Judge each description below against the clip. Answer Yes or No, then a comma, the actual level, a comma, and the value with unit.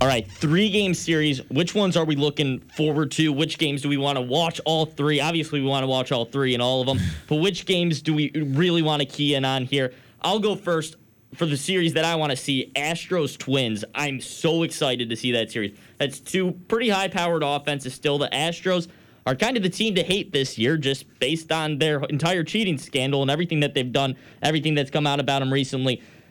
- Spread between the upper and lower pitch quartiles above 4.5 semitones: No, average, 3.7 semitones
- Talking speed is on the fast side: Yes, fast, 230 wpm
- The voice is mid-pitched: Yes, medium, 150 Hz